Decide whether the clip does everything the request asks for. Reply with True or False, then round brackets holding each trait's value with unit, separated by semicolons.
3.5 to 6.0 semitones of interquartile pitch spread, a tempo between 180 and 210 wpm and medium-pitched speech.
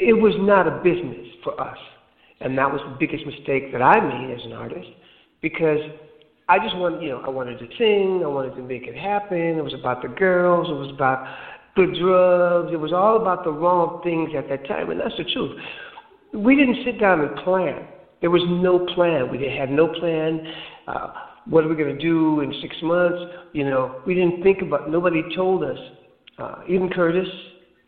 True (3.9 semitones; 205 wpm; 170 Hz)